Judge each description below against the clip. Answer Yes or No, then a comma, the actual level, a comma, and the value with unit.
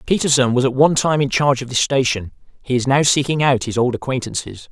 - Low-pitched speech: Yes, low, 130 Hz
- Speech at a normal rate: No, fast, 230 wpm